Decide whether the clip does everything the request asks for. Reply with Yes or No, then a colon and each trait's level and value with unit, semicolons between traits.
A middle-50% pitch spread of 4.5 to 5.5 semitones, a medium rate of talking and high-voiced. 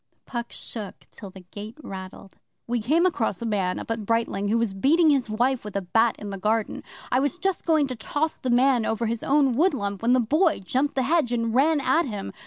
No: average, 4.8 semitones; fast, 225 wpm; high, 235 Hz